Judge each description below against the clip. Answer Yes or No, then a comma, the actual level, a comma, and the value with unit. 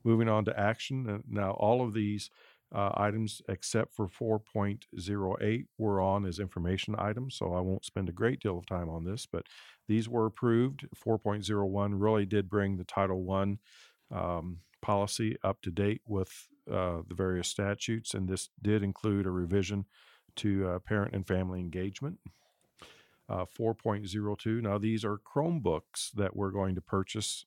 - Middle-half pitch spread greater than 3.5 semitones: No, narrow, 2.4 semitones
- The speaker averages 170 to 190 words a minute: No, average, 160 wpm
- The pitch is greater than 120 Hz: No, low, 100 Hz